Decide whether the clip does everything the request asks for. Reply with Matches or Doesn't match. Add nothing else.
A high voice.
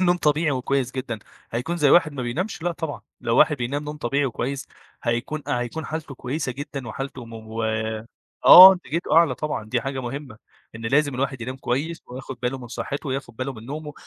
Doesn't match